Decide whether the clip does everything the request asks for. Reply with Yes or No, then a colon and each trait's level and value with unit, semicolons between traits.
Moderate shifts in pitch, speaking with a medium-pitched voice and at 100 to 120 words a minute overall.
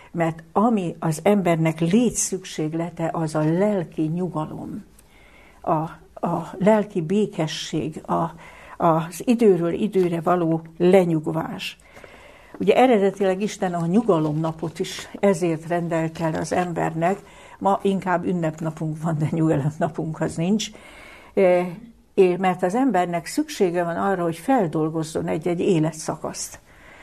Yes: average, 3.2 semitones; medium, 175 Hz; average, 110 wpm